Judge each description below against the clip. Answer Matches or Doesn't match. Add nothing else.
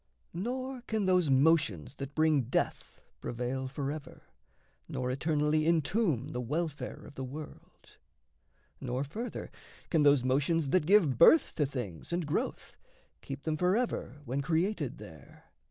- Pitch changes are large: Doesn't match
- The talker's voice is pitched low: Doesn't match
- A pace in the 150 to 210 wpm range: Doesn't match